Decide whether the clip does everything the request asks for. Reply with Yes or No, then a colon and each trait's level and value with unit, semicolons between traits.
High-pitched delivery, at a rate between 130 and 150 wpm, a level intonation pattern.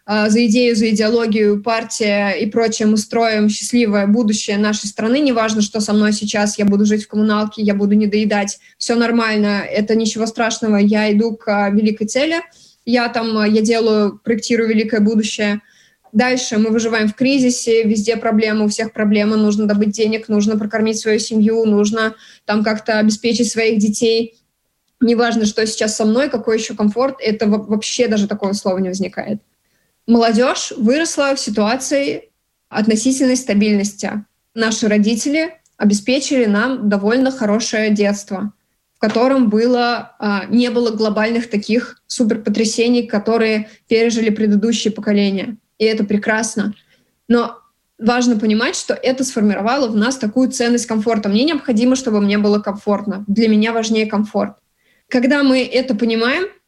Yes: high, 220 Hz; average, 145 wpm; narrow, 1.9 semitones